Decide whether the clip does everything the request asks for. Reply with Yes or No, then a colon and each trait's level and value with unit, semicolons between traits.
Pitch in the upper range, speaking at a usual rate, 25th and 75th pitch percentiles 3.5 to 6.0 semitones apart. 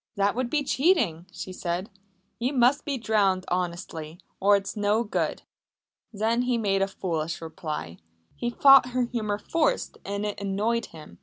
Yes: high, 205 Hz; average, 160 wpm; average, 4.7 semitones